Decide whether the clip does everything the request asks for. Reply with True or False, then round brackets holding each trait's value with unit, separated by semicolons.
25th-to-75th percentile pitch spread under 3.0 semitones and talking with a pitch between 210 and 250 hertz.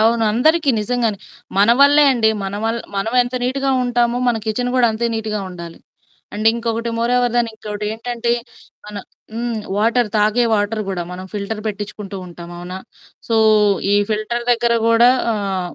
True (2.5 semitones; 225 Hz)